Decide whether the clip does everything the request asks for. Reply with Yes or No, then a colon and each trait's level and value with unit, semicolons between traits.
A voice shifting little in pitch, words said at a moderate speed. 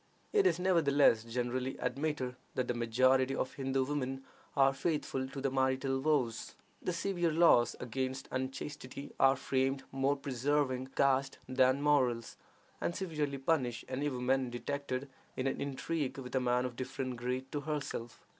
Yes: narrow, 1.9 semitones; average, 155 wpm